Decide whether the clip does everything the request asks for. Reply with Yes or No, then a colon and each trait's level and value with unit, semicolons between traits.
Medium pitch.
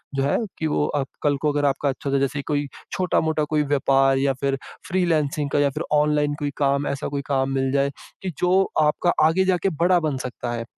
Yes: medium, 145 Hz